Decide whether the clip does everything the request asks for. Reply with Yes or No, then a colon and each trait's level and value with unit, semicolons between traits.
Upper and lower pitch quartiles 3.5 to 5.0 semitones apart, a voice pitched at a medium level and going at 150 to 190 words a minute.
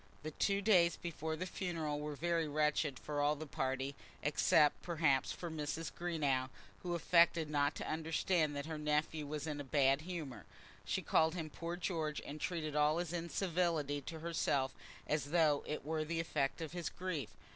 No: narrow, 2.5 semitones; medium, 155 Hz; average, 180 wpm